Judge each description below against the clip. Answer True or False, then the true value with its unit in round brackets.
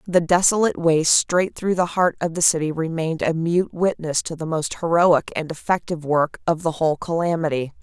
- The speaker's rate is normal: True (190 wpm)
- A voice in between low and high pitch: True (165 Hz)